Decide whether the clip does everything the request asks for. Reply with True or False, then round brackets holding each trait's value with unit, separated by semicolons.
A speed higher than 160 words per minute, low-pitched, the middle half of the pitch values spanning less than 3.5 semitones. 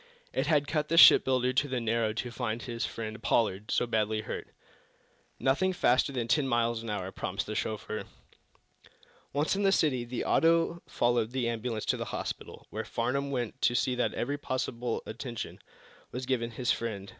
True (180 wpm; 120 Hz; 2.7 semitones)